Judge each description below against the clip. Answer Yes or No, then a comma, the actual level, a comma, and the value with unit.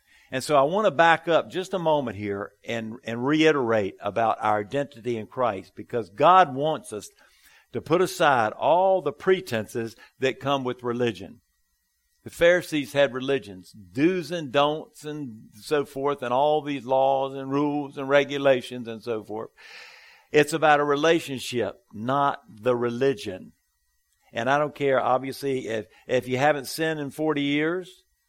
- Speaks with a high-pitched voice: No, low, 135 Hz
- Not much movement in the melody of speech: No, average, 4.3 semitones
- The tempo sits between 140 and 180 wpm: Yes, average, 155 wpm